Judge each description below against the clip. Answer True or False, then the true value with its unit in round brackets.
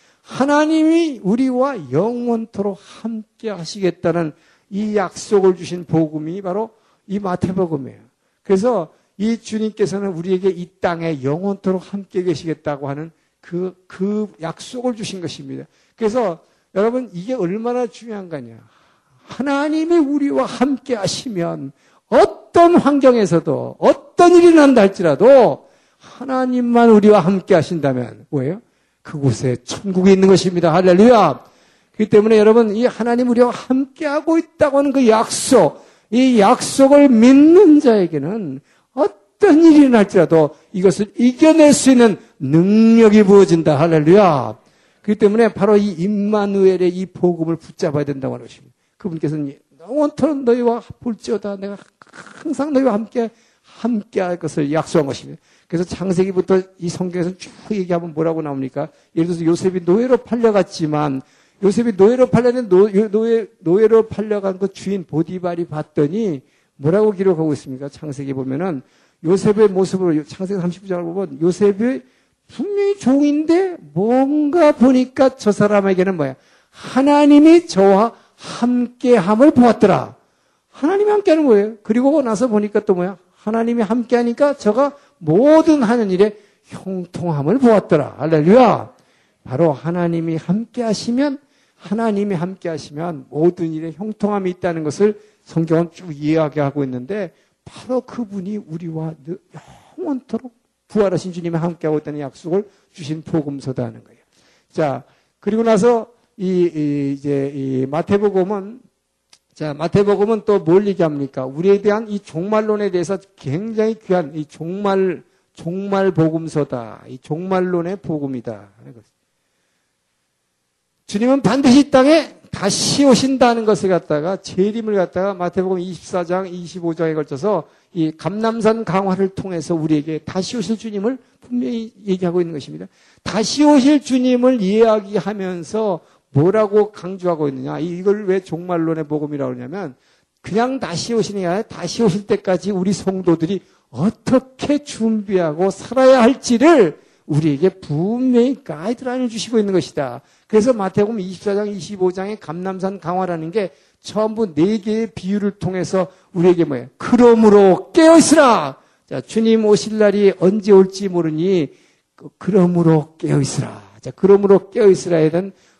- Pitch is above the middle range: True (195 Hz)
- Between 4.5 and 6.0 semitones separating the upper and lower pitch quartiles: True (5.3 semitones)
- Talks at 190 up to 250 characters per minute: False (315 characters per minute)